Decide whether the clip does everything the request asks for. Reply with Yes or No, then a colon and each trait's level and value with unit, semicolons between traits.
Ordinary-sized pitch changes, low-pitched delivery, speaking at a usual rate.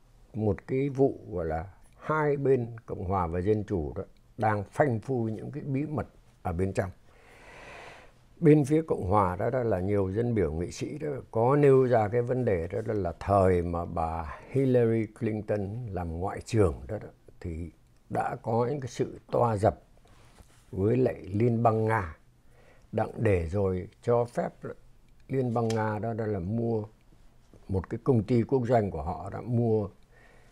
Yes: average, 3.8 semitones; low, 110 Hz; average, 180 wpm